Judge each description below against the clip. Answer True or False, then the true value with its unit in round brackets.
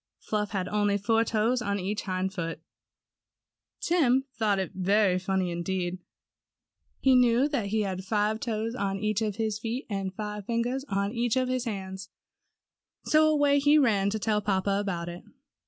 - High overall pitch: True (210 Hz)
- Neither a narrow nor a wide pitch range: True (3.4 semitones)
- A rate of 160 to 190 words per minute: True (170 wpm)